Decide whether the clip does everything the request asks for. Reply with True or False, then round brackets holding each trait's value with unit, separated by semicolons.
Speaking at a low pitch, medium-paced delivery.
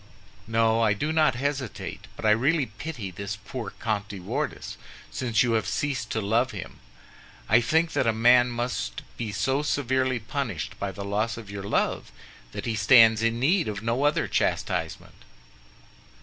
True (115 Hz; 170 wpm)